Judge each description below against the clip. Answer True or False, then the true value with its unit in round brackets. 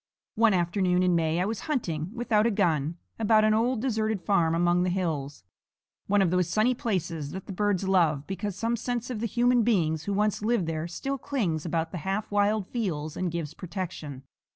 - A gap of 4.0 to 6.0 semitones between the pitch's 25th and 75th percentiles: True (4.5 semitones)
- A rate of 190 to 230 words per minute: True (200 wpm)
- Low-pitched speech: False (190 Hz)